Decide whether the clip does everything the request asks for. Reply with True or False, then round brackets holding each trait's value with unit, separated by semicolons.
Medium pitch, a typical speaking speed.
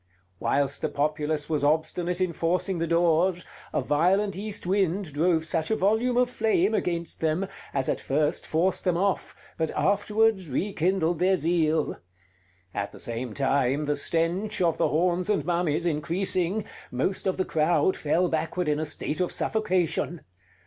True (170 Hz; 160 wpm)